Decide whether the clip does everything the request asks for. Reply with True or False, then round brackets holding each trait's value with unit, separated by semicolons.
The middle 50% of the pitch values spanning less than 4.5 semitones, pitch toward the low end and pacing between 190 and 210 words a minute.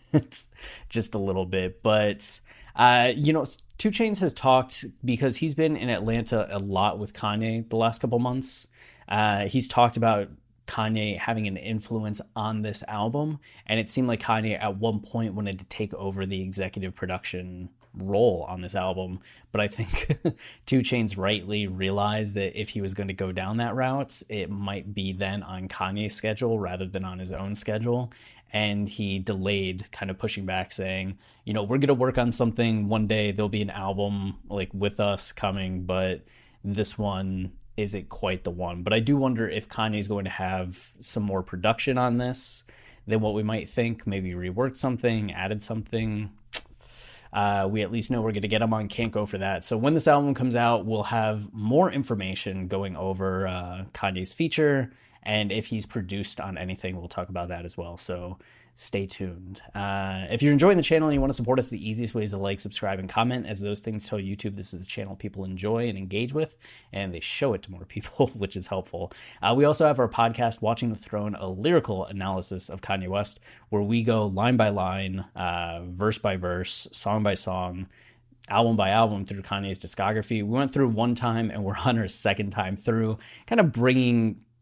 True (3.3 semitones; 105 Hz; 200 wpm)